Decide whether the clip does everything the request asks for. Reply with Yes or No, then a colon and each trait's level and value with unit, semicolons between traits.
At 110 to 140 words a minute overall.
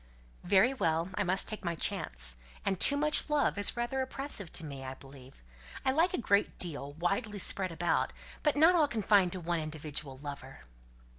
No: average, 175 wpm